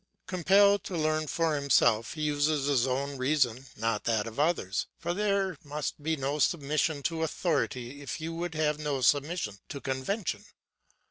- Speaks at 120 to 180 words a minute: Yes, average, 160 wpm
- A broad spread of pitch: No, average, 3.7 semitones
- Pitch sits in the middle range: Yes, medium, 150 Hz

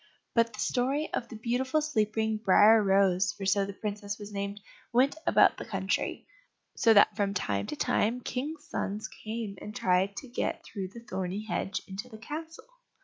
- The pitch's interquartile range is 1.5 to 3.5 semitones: Yes, average, 3.1 semitones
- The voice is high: Yes, high, 215 Hz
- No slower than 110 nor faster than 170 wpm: No, average, 180 wpm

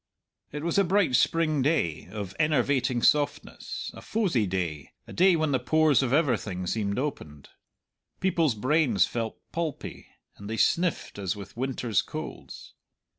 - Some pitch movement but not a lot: No, wide, 7.4 semitones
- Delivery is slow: No, average, 145 wpm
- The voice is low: Yes, low, 130 Hz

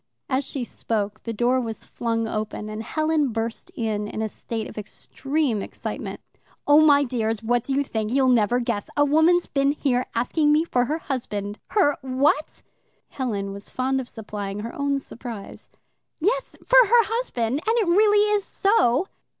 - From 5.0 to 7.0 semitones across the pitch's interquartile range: Yes, average, 5.3 semitones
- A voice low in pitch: No, very high, 255 Hz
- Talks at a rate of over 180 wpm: No, average, 175 wpm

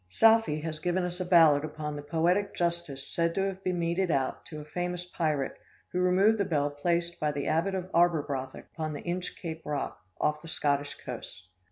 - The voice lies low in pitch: No, medium, 170 Hz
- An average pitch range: Yes, average, 3.1 semitones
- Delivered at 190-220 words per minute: Yes, average, 195 wpm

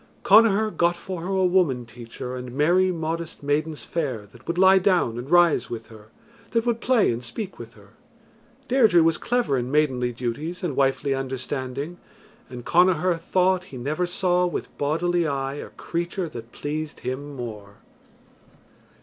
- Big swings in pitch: Yes, wide, 5.9 semitones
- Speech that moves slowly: No, average, 160 wpm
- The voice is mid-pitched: Yes, medium, 155 Hz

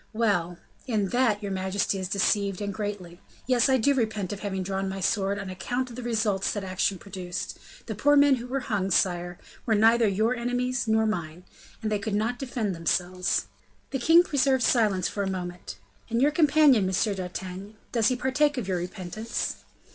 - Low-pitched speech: No, high, 205 Hz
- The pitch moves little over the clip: No, average, 4.5 semitones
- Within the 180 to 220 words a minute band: Yes, average, 190 wpm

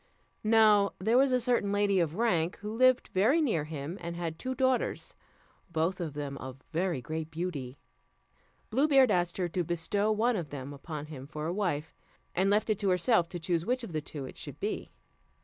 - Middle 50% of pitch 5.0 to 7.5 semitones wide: Yes, wide, 5.4 semitones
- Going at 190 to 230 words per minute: Yes, average, 200 wpm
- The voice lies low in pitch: No, medium, 180 Hz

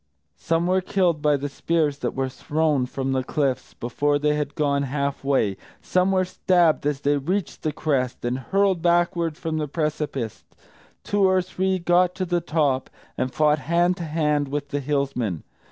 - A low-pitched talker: No, medium, 150 Hz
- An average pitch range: Yes, average, 3.7 semitones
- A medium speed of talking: Yes, average, 180 wpm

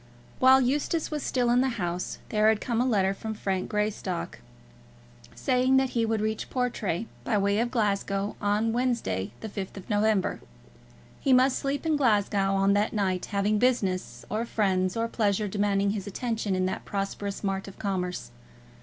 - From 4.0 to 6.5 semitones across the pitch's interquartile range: No, average, 3.5 semitones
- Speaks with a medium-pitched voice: No, high, 210 Hz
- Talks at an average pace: Yes, average, 170 wpm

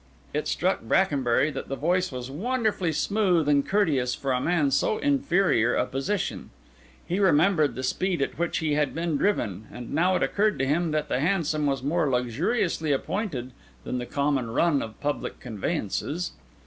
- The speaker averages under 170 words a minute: No, average, 175 wpm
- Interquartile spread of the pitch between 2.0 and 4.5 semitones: No, wide, 5.4 semitones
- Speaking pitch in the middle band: Yes, medium, 150 Hz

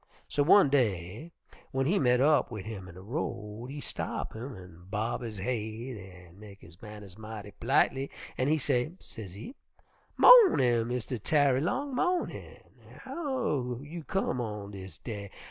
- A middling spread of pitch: No, wide, 5.7 semitones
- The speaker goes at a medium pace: Yes, average, 155 wpm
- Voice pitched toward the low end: Yes, low, 120 Hz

